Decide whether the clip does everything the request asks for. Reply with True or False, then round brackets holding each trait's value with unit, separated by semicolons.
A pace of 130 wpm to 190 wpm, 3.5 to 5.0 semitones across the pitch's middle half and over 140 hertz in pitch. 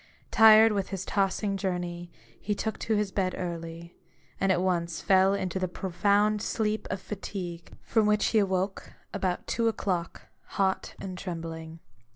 False (155 wpm; 2.9 semitones; 190 Hz)